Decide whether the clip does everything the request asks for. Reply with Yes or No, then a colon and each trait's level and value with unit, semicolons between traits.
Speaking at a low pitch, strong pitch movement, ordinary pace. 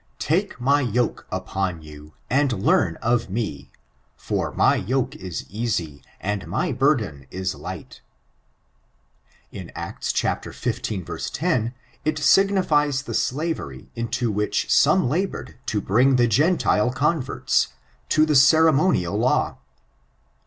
No: low, 120 Hz; wide, 7.3 semitones; slow, 115 wpm